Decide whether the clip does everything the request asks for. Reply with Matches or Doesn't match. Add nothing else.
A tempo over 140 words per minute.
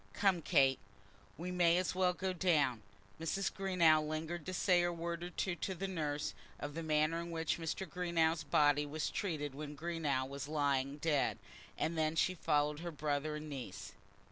Matches